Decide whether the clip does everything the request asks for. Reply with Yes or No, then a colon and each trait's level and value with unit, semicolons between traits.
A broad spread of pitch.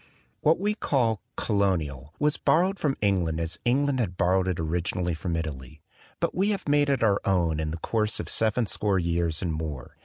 Yes: wide, 7.6 semitones